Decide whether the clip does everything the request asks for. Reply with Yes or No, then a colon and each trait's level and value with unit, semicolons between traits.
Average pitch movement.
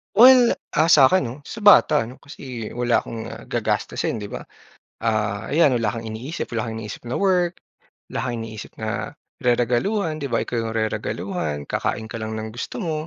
No: wide, 6.1 semitones